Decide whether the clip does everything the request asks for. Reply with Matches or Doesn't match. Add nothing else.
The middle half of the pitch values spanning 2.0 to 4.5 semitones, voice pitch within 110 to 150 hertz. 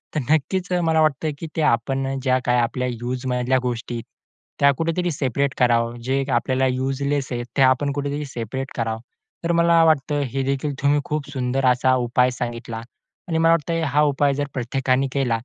Matches